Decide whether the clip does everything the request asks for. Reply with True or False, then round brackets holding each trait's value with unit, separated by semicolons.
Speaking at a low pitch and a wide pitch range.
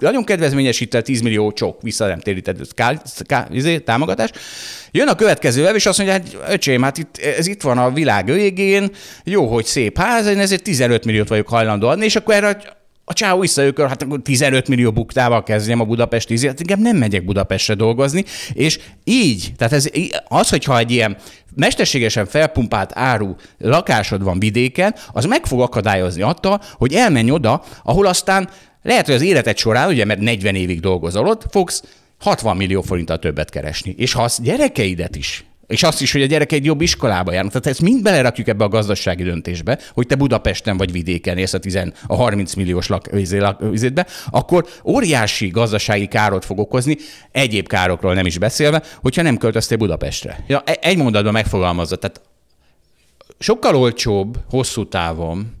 True (120 Hz; 7.6 semitones)